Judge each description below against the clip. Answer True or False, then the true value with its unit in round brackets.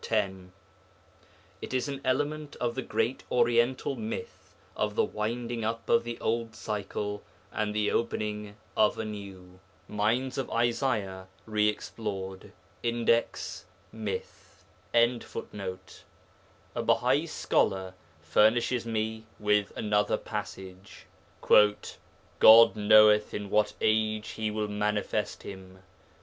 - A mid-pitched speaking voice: False (110 Hz)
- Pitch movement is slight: True (2.2 semitones)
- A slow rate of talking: True (115 wpm)